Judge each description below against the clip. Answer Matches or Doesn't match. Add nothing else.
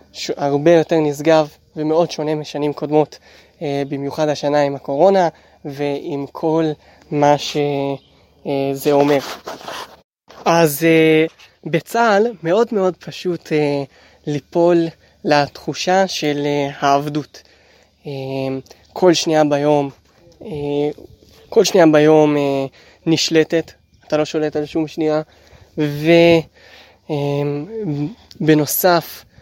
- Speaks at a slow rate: Matches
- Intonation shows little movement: Matches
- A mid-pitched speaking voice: Matches